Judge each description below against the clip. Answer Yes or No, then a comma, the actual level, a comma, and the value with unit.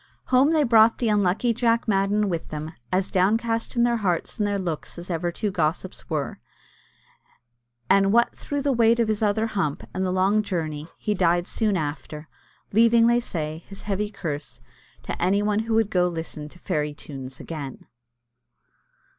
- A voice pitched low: No, high, 195 Hz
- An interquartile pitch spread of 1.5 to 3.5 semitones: No, average, 5.1 semitones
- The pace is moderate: Yes, average, 180 wpm